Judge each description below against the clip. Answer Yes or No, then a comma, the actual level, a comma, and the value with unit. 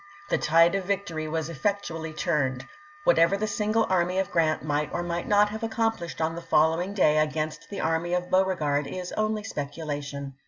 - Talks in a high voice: No, medium, 170 Hz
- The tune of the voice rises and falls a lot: No, average, 4.3 semitones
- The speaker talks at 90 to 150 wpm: No, average, 180 wpm